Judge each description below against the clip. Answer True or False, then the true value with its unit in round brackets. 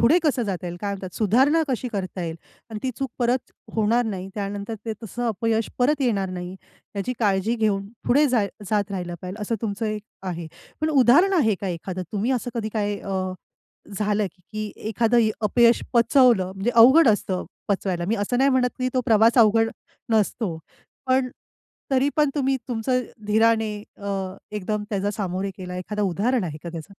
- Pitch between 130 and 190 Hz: False (215 Hz)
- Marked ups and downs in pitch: False (3.8 semitones)